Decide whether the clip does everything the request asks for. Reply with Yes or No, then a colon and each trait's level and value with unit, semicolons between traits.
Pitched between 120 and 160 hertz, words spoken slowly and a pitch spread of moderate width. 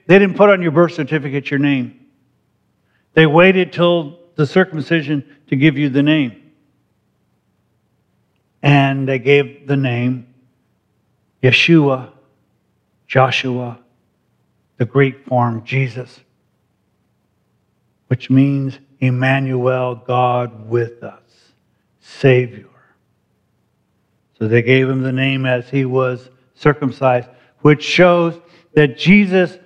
Yes: low, 135 Hz; slow, 105 wpm; average, 3.2 semitones